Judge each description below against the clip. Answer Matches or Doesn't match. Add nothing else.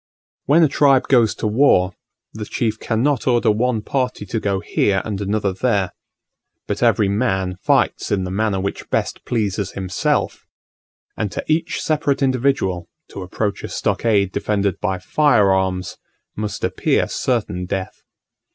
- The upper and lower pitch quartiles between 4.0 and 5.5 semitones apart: Matches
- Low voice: Matches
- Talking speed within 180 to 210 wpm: Doesn't match